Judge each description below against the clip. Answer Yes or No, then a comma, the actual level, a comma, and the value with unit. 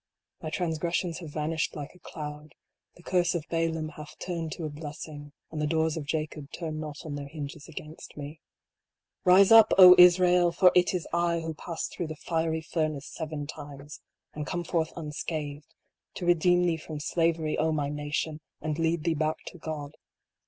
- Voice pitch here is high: No, medium, 160 Hz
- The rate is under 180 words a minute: No, average, 185 wpm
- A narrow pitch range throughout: Yes, narrow, 2.2 semitones